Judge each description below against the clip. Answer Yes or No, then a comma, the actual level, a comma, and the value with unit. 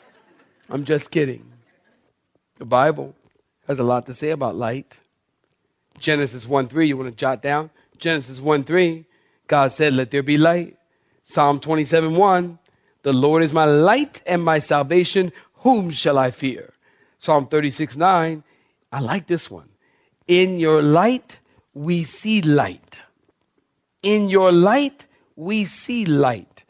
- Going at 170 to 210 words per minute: No, average, 140 wpm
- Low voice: No, medium, 155 Hz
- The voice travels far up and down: No, average, 3.8 semitones